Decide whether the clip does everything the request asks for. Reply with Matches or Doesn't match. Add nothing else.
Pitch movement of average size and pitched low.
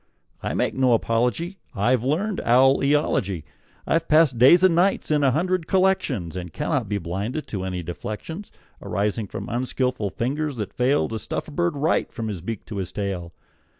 Doesn't match